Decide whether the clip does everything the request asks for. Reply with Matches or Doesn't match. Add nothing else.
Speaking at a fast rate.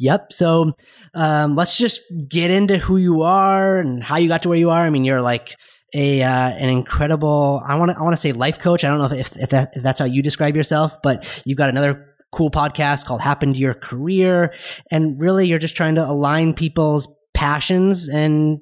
Matches